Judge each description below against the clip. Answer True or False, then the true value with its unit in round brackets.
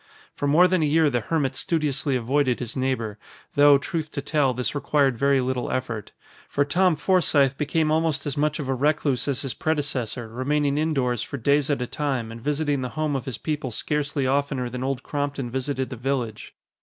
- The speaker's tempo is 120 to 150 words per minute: False (195 wpm)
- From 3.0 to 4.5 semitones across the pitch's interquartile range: False (2.6 semitones)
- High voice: False (140 Hz)